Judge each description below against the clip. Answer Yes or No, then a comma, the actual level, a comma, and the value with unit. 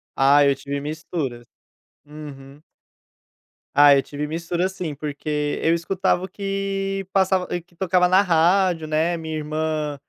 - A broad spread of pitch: No, average, 3.7 semitones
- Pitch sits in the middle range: Yes, medium, 160 Hz